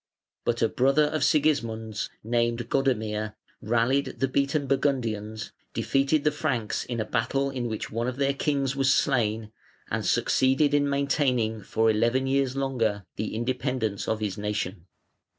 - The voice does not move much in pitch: No, average, 3.7 semitones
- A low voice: Yes, low, 125 Hz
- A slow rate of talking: No, average, 150 wpm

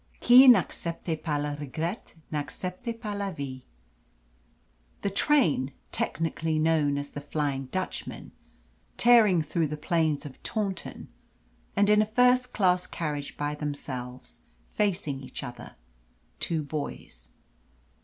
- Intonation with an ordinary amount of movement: No, wide, 5.7 semitones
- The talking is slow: Yes, slow, 120 wpm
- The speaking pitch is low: No, medium, 160 Hz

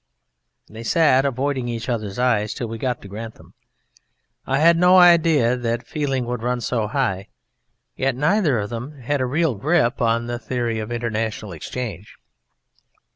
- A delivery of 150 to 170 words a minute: Yes, average, 160 wpm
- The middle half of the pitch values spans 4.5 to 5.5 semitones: No, average, 3.6 semitones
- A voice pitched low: Yes, low, 120 Hz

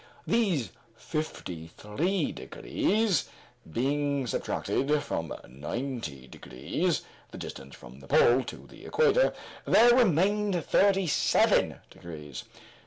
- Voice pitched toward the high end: No, medium, 145 Hz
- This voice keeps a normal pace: No, slow, 105 wpm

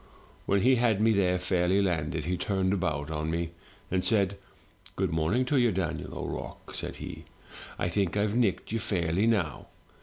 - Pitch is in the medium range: No, very low, 95 Hz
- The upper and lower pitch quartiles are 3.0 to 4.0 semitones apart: Yes, average, 3.5 semitones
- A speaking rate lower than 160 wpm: No, average, 175 wpm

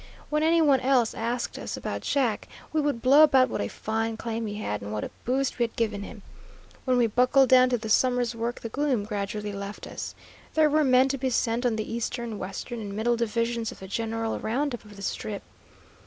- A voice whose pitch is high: Yes, high, 235 Hz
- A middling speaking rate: No, fast, 225 wpm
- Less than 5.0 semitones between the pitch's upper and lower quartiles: Yes, average, 3.0 semitones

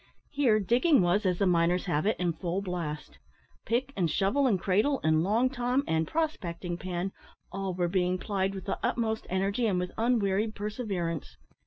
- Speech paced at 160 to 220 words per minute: Yes, average, 175 wpm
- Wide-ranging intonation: No, average, 4.2 semitones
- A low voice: No, high, 195 Hz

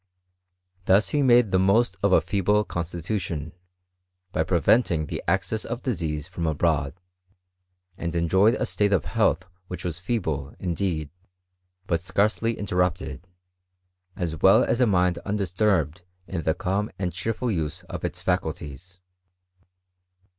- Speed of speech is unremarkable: No, slow, 130 wpm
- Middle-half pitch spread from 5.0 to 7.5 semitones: No, average, 3.5 semitones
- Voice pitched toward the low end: Yes, very low, 90 Hz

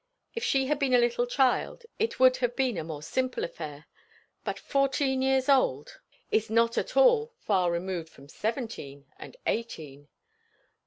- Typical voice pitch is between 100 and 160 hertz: No, high, 240 Hz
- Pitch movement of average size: No, wide, 7.8 semitones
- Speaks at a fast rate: No, average, 160 wpm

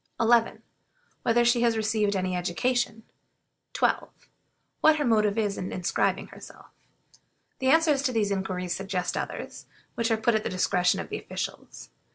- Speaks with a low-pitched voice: No, high, 220 Hz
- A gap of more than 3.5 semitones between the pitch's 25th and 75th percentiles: Yes, average, 3.9 semitones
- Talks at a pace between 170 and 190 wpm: No, average, 155 wpm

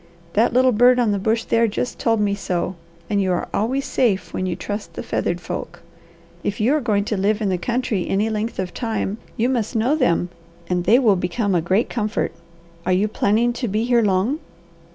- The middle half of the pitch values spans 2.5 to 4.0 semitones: Yes, average, 3.5 semitones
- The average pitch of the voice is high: Yes, high, 215 Hz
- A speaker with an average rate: No, fast, 215 wpm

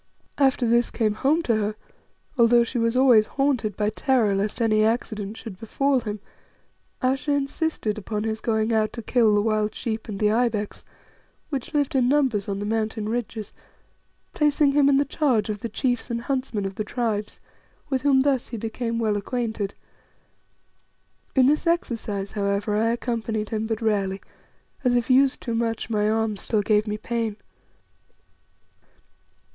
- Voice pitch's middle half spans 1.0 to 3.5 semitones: Yes, average, 3.1 semitones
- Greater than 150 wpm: Yes, average, 165 wpm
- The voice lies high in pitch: Yes, high, 225 Hz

